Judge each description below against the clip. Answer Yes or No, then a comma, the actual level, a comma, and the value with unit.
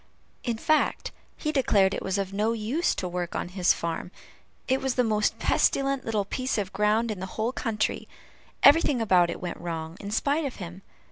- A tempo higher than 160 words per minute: Yes, average, 195 wpm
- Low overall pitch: No, high, 210 Hz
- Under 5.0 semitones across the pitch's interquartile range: No, wide, 5.5 semitones